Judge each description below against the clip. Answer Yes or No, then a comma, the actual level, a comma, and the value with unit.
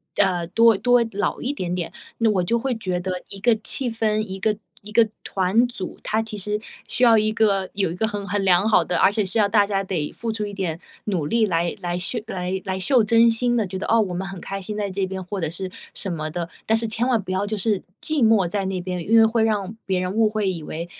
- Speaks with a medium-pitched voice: No, high, 200 Hz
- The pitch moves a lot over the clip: No, average, 3.2 semitones